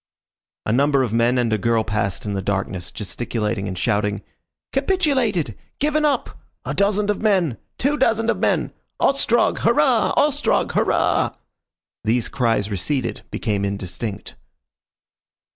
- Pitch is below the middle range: Yes, low, 120 Hz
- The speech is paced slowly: Yes, slow, 130 wpm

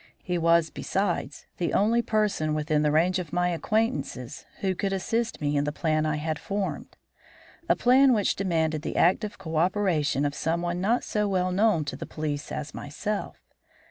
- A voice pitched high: No, medium, 175 Hz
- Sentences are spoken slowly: No, average, 175 wpm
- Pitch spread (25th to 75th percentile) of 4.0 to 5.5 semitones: Yes, average, 4.7 semitones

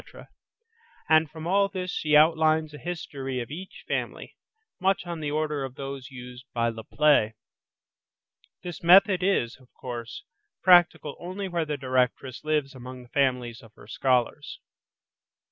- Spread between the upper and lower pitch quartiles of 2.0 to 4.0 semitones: No, average, 5.0 semitones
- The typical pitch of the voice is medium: Yes, medium, 150 Hz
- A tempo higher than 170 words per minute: No, average, 145 wpm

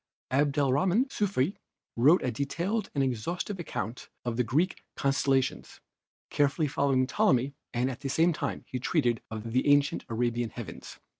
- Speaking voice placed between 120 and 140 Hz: Yes, low, 135 Hz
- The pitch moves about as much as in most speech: Yes, average, 4.3 semitones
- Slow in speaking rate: No, average, 145 wpm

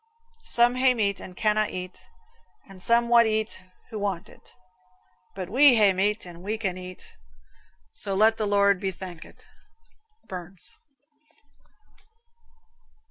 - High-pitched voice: Yes, high, 200 Hz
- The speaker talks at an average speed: No, slow, 130 wpm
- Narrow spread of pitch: No, average, 3.1 semitones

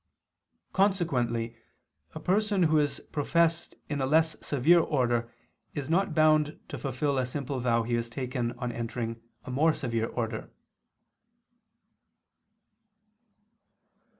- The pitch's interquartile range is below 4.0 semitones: No, average, 4.9 semitones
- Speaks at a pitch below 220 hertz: Yes, medium, 140 Hz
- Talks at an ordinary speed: No, slow, 120 wpm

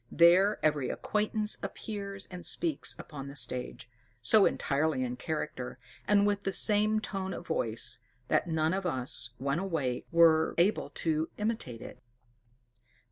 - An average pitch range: No, wide, 6.1 semitones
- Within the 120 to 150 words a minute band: Yes, average, 140 wpm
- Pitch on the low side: No, medium, 165 Hz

